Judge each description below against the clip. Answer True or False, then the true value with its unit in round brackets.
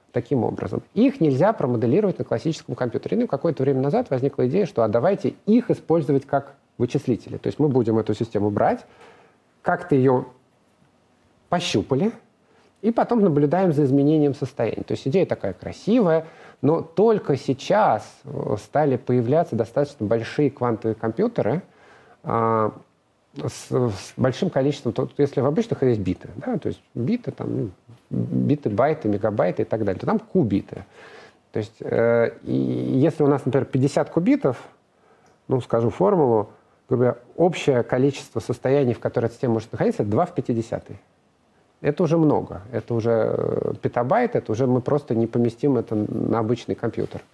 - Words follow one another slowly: False (150 wpm)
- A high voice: False (135 Hz)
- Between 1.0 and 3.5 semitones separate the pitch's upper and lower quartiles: False (4.8 semitones)